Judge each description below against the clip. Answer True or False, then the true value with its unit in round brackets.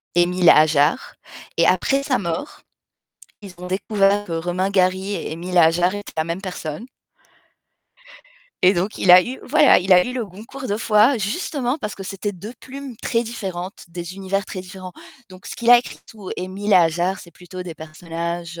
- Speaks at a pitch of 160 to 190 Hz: True (185 Hz)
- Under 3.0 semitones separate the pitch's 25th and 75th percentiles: False (3.3 semitones)